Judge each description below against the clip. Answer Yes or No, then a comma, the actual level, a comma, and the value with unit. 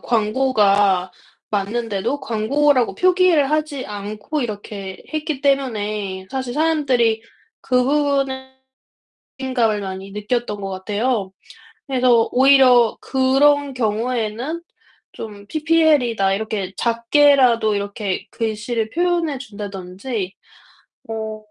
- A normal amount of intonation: Yes, average, 4.8 semitones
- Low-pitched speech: No, high, 235 Hz